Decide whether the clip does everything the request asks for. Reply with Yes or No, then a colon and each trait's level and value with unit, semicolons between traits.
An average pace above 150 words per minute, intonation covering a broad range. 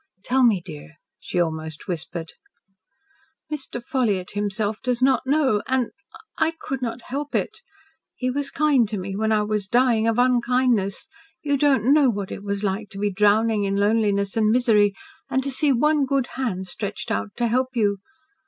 No: average, 175 wpm; average, 4.4 semitones